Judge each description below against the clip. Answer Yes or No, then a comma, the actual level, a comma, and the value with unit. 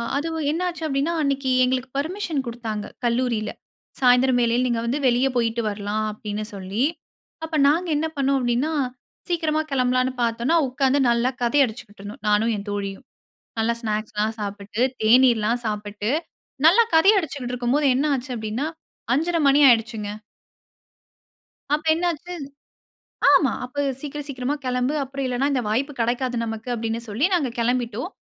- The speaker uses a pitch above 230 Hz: Yes, very high, 250 Hz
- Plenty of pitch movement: No, average, 3.9 semitones